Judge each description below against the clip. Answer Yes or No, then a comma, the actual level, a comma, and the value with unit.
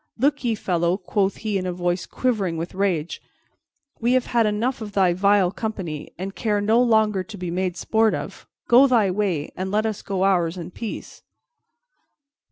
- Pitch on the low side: No, high, 200 Hz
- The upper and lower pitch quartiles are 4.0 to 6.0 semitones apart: No, average, 3.5 semitones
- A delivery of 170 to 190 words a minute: Yes, average, 180 wpm